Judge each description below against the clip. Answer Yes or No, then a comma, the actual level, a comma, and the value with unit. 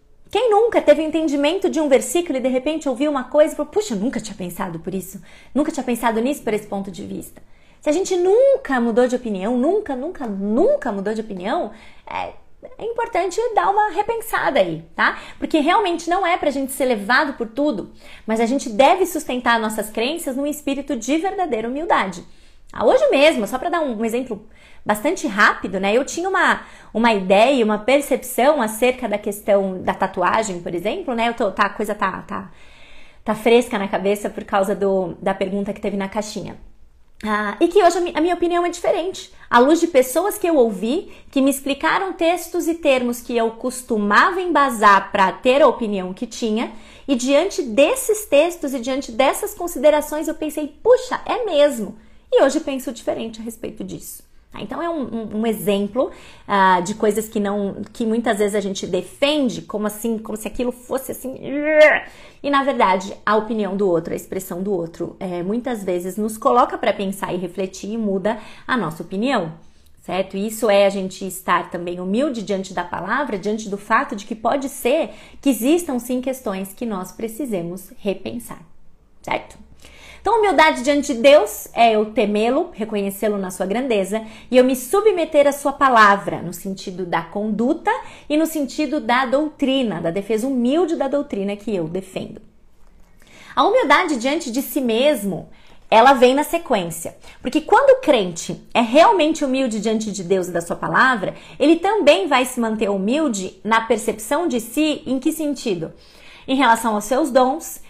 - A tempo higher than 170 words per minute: Yes, fast, 185 wpm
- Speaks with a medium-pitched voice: No, high, 245 Hz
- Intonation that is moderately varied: No, wide, 6.3 semitones